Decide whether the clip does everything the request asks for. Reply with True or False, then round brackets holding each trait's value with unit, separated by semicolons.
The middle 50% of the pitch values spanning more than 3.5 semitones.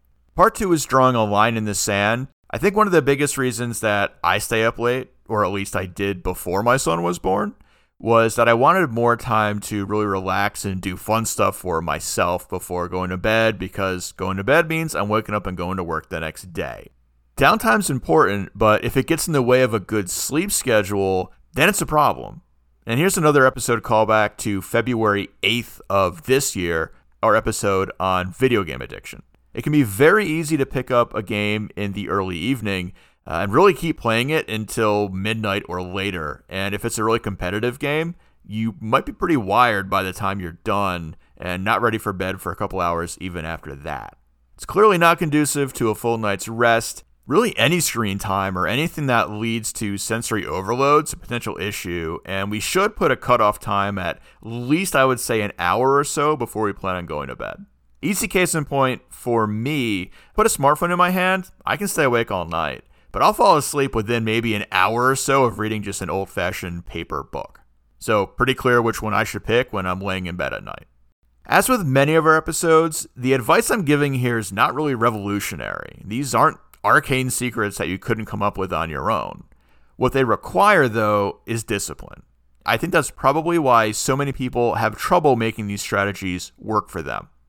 True (5.4 semitones)